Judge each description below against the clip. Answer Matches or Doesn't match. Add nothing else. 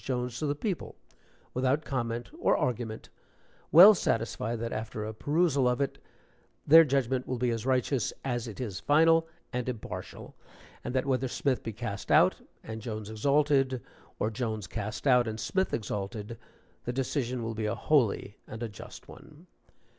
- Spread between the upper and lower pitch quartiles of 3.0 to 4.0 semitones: Matches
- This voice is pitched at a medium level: Doesn't match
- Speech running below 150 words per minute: Doesn't match